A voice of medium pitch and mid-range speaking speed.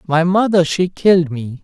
Yes: medium, 170 Hz; average, 185 wpm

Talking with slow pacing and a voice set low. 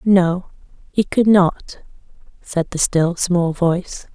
No: slow, 130 wpm; medium, 180 Hz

